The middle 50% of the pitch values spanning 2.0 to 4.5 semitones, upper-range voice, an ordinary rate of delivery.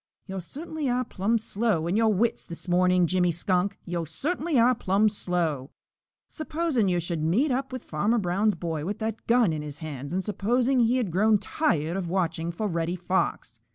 No: wide, 5.4 semitones; high, 195 Hz; average, 190 wpm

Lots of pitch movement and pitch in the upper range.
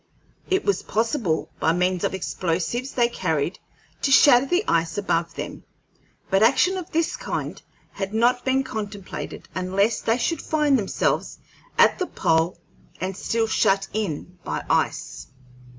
Yes: wide, 6.2 semitones; high, 215 Hz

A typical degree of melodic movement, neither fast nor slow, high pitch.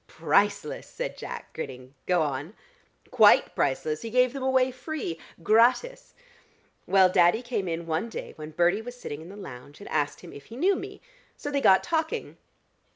No: wide, 8.2 semitones; average, 175 wpm; high, 205 Hz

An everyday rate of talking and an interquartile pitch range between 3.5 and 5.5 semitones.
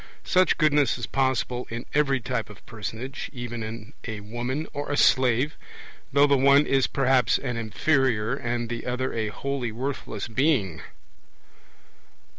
No: average, 145 wpm; average, 3.1 semitones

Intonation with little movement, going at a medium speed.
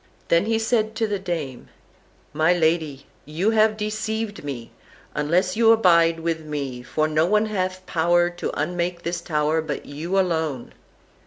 No: average, 4.6 semitones; average, 155 wpm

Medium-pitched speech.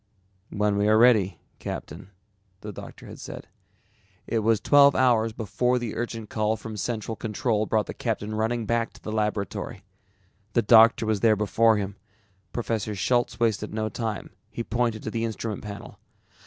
No: low, 110 Hz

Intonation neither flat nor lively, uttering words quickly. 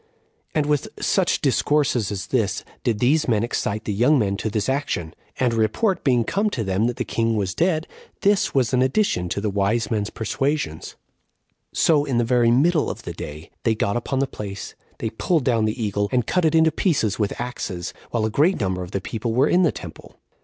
No: wide, 5.7 semitones; fast, 215 wpm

